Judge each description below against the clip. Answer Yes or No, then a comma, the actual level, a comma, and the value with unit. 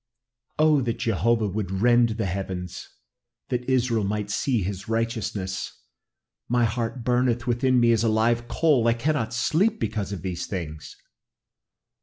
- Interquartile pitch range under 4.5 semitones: Yes, average, 3.4 semitones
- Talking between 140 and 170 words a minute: Yes, average, 145 wpm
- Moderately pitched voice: No, low, 115 Hz